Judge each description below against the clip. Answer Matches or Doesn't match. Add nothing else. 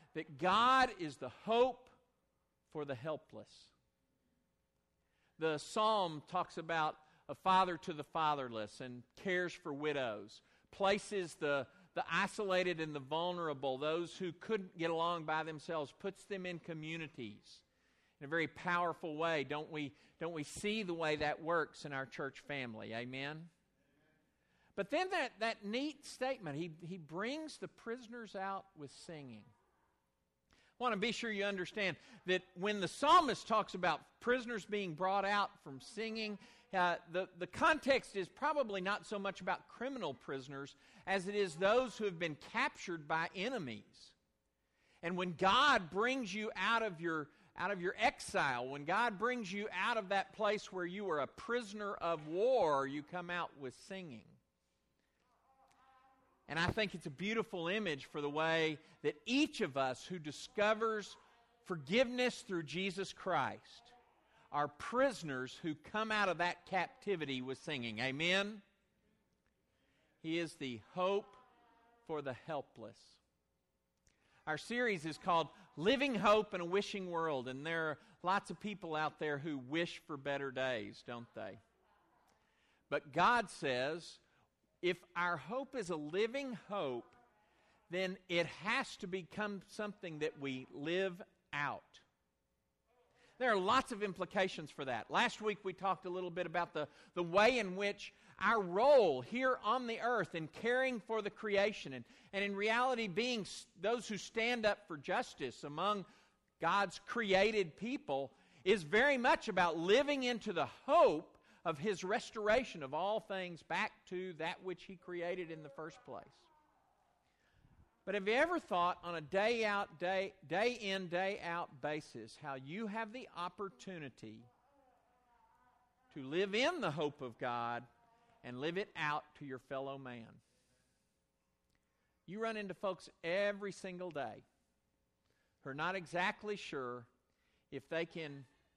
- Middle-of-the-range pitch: Matches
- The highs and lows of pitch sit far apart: Matches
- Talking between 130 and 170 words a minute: Matches